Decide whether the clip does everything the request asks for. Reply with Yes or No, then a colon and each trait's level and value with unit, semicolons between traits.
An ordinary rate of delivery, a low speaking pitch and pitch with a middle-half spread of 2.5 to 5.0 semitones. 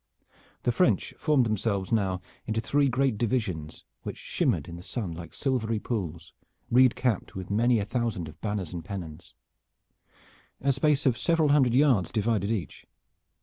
No: average, 155 wpm; low, 110 Hz; wide, 5.5 semitones